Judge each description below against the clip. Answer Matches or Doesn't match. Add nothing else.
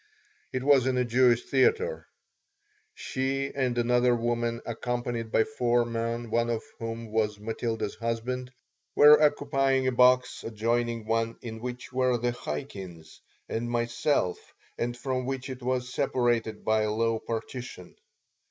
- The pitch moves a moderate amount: Doesn't match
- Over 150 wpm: Doesn't match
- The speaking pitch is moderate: Doesn't match